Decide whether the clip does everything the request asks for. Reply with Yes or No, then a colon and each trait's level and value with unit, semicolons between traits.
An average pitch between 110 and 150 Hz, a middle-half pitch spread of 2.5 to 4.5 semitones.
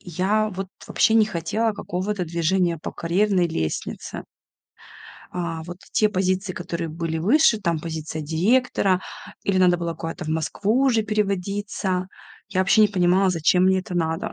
No: medium, 185 Hz; average, 3.3 semitones